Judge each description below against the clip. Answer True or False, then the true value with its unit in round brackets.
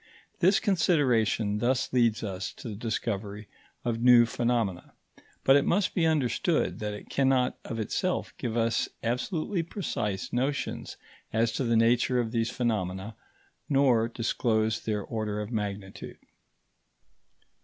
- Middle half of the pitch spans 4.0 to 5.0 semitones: False (3.2 semitones)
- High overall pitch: False (115 Hz)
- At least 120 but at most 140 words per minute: True (135 wpm)